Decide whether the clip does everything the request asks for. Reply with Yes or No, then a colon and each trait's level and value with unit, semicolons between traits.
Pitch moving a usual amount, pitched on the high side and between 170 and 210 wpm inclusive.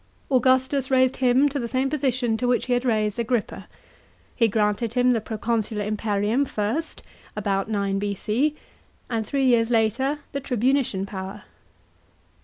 No: average, 3.7 semitones; high, 235 Hz; average, 150 wpm